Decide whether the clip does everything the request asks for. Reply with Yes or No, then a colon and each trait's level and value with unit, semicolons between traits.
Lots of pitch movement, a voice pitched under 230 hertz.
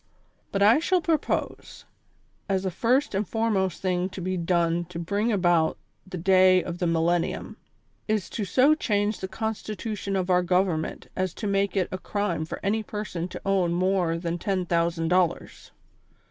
No: average, 2.9 semitones; medium, 185 Hz